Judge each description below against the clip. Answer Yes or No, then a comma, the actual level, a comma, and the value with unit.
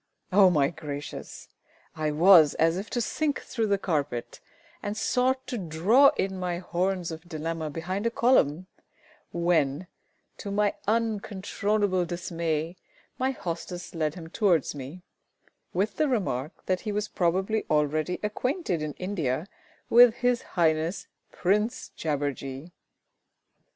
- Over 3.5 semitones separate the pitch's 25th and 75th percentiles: Yes, average, 4.8 semitones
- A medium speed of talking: No, slow, 130 wpm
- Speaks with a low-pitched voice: No, medium, 180 Hz